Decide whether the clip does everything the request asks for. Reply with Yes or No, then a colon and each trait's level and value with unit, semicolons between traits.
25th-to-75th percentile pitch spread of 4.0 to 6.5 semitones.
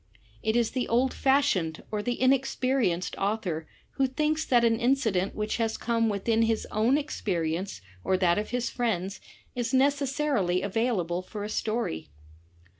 Yes: average, 5.2 semitones